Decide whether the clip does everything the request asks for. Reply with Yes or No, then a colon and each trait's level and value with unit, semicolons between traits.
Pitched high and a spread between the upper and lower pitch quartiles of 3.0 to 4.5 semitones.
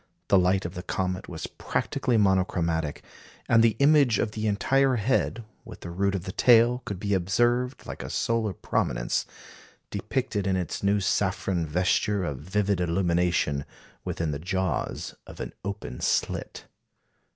No: very low, 95 Hz; average, 3.7 semitones